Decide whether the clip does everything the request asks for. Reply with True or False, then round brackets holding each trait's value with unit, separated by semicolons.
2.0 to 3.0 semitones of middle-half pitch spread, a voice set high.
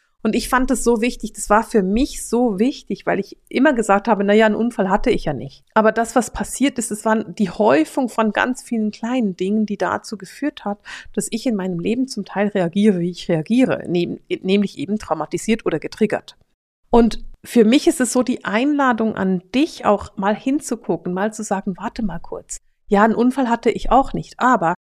False (3.6 semitones; 220 Hz)